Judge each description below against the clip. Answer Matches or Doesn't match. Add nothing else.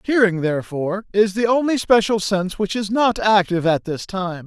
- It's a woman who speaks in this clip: Doesn't match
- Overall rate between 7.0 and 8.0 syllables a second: Doesn't match